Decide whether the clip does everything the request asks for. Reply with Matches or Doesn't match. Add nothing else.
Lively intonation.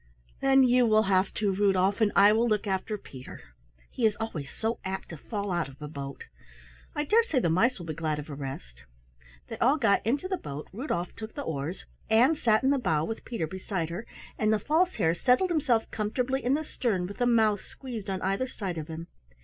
Matches